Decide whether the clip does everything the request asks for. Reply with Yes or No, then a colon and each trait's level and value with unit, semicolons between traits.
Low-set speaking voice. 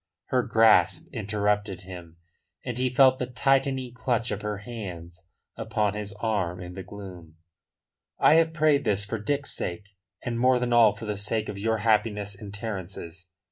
Yes: low, 105 Hz